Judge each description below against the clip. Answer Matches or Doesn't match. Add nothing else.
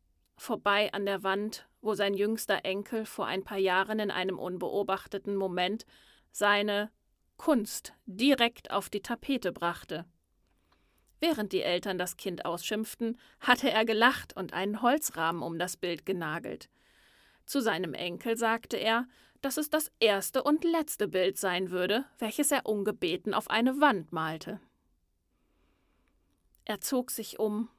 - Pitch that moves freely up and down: Doesn't match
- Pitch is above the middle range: Matches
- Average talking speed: Matches